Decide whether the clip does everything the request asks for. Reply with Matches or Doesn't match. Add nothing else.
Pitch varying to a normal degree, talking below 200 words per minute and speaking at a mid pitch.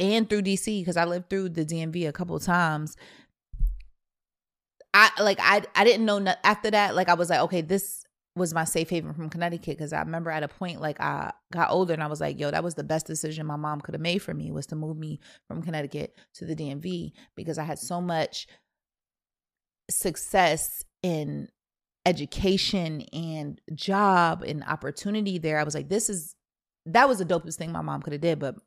Doesn't match